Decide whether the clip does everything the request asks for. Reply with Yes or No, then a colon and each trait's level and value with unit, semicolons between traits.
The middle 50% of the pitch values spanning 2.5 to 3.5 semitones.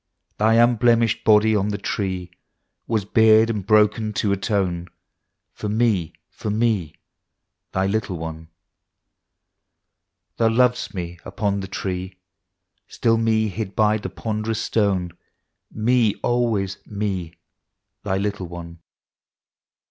Yes: average, 2.9 semitones